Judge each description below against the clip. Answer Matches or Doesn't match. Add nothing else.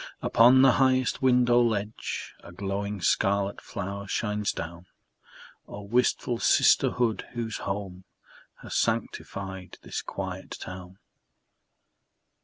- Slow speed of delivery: Matches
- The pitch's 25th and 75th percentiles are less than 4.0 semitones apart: Matches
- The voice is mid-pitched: Doesn't match